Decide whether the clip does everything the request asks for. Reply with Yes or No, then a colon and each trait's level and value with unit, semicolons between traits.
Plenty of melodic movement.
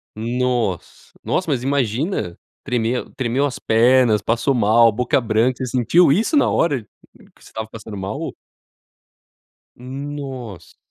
No: average, 3.5 semitones